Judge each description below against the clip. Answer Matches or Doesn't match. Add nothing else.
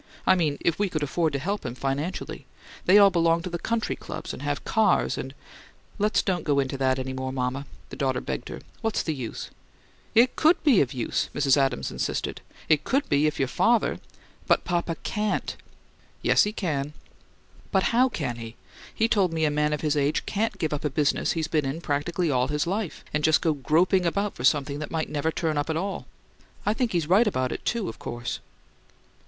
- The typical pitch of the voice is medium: Matches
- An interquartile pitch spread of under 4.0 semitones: Doesn't match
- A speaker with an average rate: Doesn't match